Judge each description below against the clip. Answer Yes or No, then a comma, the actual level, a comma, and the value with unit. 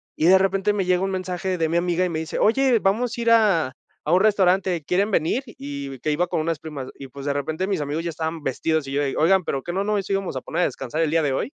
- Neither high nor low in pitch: Yes, medium, 170 Hz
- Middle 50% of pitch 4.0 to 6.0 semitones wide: Yes, average, 4.3 semitones